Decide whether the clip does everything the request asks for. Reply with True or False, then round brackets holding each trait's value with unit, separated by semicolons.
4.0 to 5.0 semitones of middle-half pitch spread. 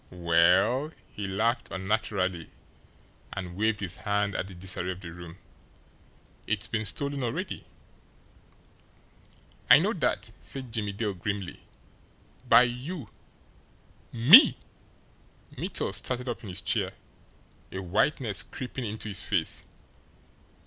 True (4.3 semitones)